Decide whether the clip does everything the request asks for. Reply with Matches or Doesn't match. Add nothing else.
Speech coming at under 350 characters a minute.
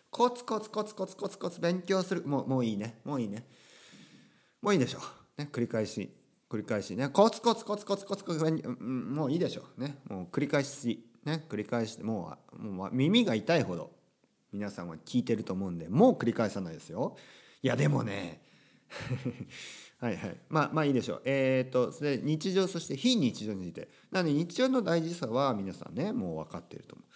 Doesn't match